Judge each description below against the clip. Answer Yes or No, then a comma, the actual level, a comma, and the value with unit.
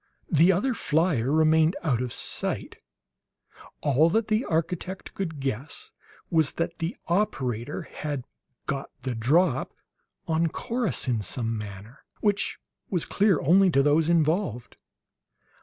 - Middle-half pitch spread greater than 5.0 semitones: Yes, wide, 5.6 semitones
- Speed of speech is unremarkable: No, slow, 125 wpm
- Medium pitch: Yes, medium, 160 Hz